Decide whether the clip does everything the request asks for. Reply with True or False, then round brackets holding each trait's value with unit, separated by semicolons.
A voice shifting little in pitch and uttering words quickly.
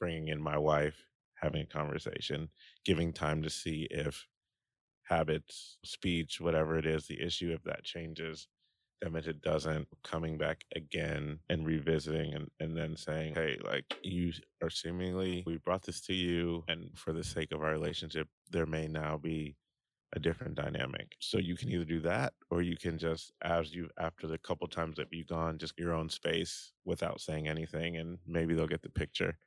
False (1.4 semitones; 185 wpm)